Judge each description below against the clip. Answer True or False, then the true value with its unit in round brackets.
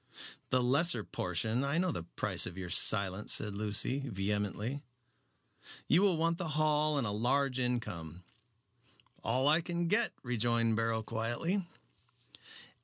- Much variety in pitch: True (6.4 semitones)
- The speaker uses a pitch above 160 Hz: False (125 Hz)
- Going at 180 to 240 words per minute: False (135 wpm)